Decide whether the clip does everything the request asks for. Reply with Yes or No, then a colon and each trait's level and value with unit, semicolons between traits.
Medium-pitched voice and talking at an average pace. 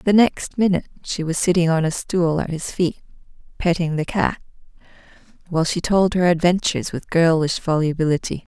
Yes: medium, 170 Hz; average, 170 wpm